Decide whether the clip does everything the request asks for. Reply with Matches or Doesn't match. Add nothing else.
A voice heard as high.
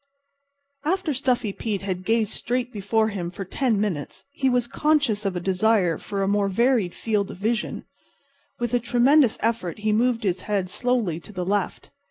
Matches